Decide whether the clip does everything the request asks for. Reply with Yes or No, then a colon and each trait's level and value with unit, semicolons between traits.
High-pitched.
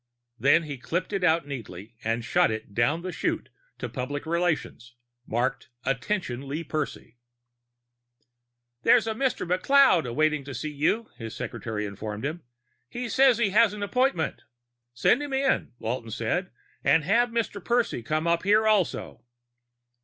No: medium, 160 Hz